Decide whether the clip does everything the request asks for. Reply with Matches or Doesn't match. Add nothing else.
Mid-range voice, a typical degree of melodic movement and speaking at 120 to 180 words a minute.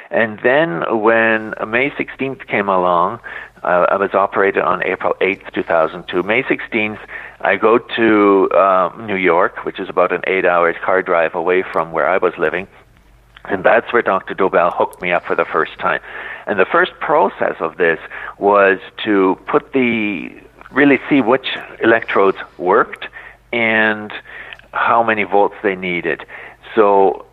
Doesn't match